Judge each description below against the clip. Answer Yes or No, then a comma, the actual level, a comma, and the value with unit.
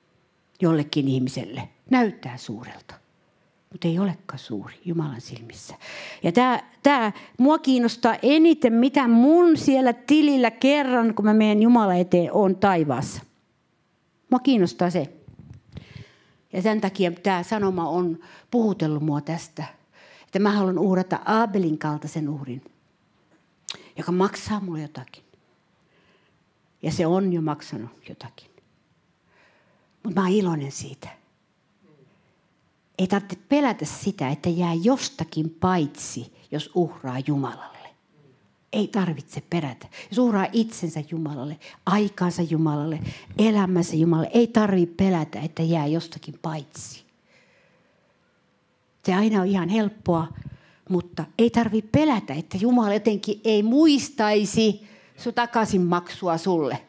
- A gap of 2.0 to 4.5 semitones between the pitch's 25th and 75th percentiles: No, wide, 5.5 semitones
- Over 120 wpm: No, average, 115 wpm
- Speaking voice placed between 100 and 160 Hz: No, medium, 180 Hz